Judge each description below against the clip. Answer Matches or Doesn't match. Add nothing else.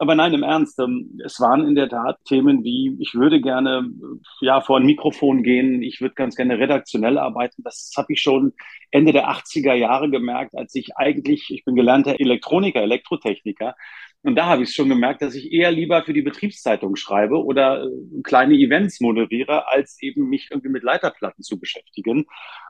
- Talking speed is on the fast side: Doesn't match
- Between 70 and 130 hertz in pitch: Doesn't match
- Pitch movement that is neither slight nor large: Doesn't match